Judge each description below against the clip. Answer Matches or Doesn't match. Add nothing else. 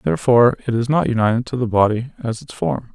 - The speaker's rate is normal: Doesn't match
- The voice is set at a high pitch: Doesn't match